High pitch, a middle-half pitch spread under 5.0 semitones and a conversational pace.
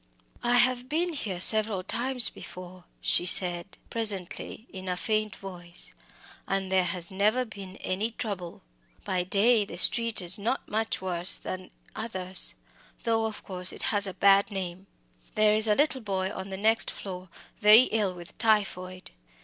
Yes: high, 200 Hz; average, 3.2 semitones; average, 160 wpm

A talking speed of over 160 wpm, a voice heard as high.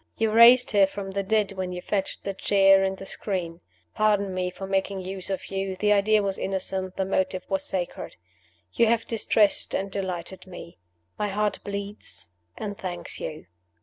Yes: average, 180 wpm; high, 195 Hz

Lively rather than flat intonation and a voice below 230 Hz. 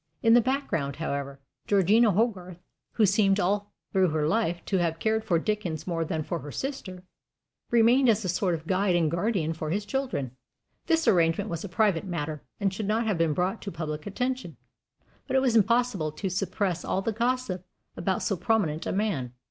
No: average, 5.0 semitones; high, 190 Hz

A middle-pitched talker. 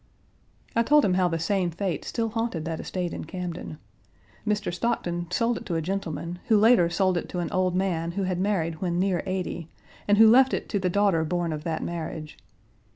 Yes: medium, 180 Hz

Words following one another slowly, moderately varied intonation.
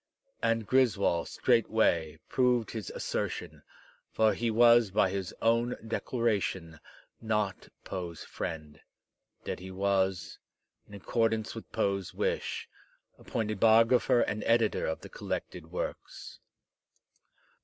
Yes: slow, 110 wpm; average, 3.4 semitones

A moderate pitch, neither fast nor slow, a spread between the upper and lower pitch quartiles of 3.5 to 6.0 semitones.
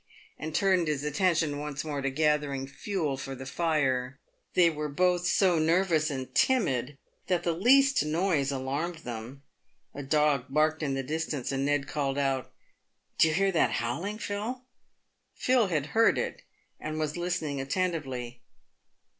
Yes: medium, 150 Hz; average, 155 wpm; average, 4.4 semitones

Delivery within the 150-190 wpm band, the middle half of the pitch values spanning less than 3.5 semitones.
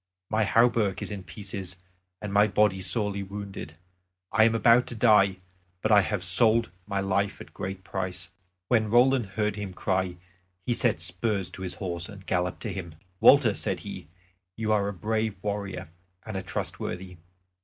Yes: average, 175 wpm; narrow, 2.6 semitones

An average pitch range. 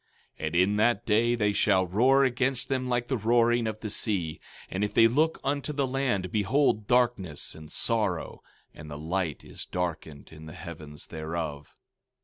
No: wide, 6.4 semitones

